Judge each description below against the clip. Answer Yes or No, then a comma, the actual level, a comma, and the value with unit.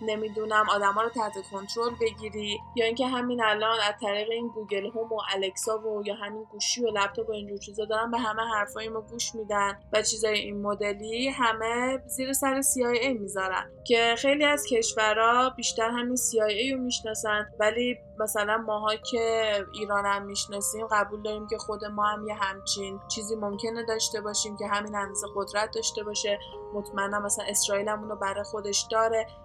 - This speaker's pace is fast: Yes, fast, 170 wpm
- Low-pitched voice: No, high, 215 Hz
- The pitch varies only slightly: Yes, narrow, 1.7 semitones